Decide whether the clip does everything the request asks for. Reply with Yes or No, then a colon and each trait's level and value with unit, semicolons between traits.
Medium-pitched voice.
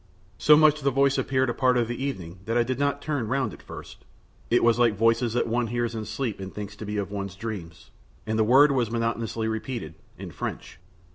No: low, 115 Hz